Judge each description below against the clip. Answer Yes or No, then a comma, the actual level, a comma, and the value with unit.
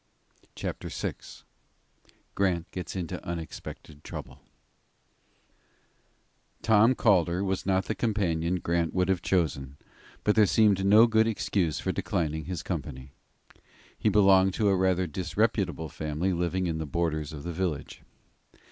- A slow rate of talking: Yes, slow, 130 wpm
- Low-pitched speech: Yes, very low, 90 Hz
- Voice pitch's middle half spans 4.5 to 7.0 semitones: No, average, 3.3 semitones